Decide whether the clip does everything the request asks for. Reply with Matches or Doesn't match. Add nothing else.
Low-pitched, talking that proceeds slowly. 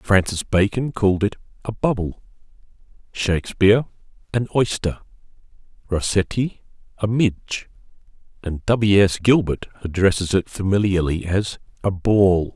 Matches